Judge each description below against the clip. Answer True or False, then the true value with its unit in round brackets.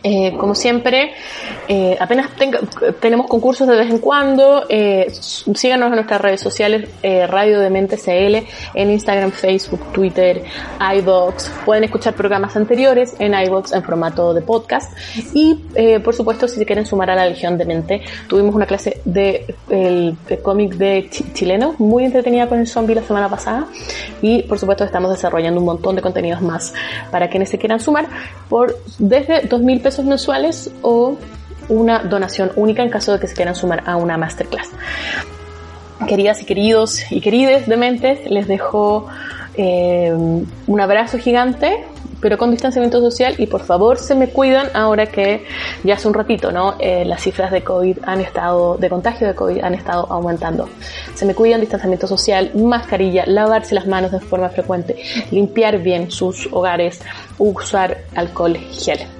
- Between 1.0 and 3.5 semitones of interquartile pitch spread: False (4.0 semitones)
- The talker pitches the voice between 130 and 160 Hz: False (205 Hz)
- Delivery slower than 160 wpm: False (165 wpm)